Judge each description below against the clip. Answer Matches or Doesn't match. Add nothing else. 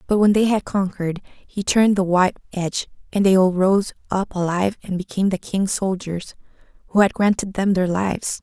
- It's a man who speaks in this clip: Doesn't match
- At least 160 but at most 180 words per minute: Doesn't match